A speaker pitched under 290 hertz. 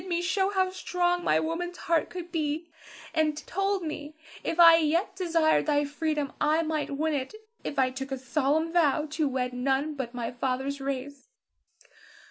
No: very high, 310 Hz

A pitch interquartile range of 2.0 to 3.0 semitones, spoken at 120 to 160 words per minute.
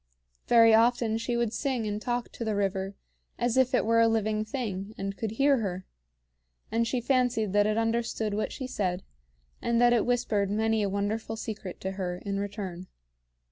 No: average, 2.7 semitones; average, 185 wpm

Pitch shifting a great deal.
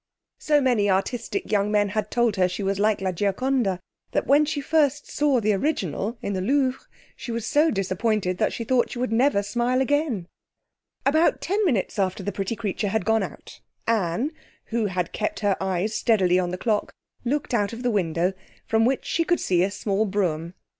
No: average, 4.9 semitones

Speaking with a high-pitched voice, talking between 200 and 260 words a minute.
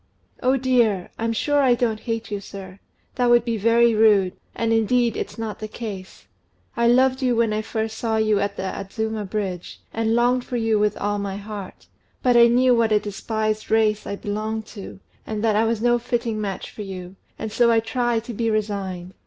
Yes: high, 220 Hz; fast, 205 wpm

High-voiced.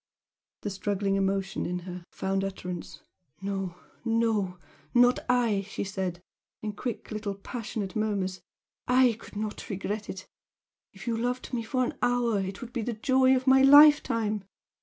Yes: high, 210 Hz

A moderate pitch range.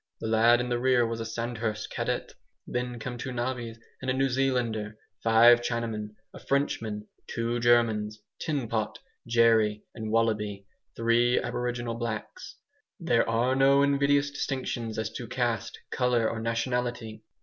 No: narrow, 1.7 semitones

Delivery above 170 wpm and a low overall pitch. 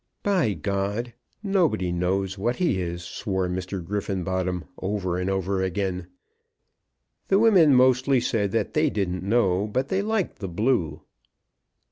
No: slow, 135 wpm; low, 100 Hz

